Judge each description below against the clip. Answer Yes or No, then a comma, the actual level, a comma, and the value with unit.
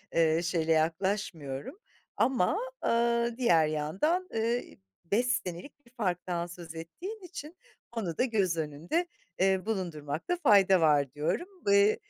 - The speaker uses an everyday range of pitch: No, wide, 6.5 semitones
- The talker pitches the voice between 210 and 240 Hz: No, high, 190 Hz